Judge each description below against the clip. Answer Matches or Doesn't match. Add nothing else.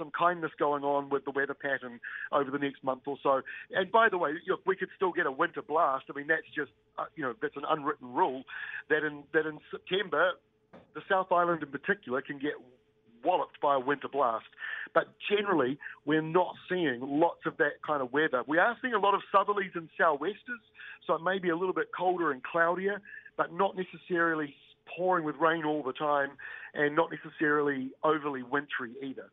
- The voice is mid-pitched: Matches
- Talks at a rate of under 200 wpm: Doesn't match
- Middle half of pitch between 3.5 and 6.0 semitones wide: Matches